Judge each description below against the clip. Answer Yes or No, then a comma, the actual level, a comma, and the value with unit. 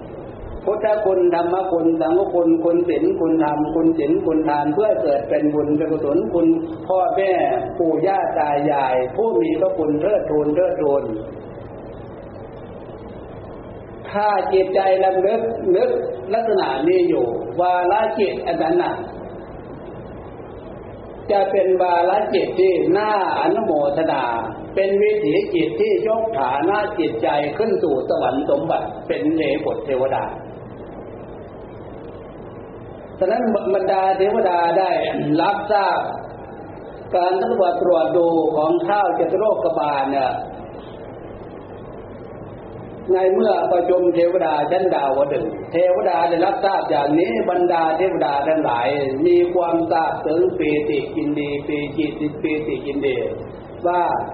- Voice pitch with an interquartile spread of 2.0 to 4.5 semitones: No, average, 5.0 semitones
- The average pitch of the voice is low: No, medium, 180 Hz